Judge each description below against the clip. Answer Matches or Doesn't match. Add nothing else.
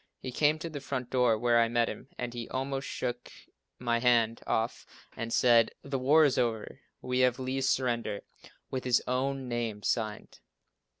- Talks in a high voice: Doesn't match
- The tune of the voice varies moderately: Doesn't match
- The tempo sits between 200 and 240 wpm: Doesn't match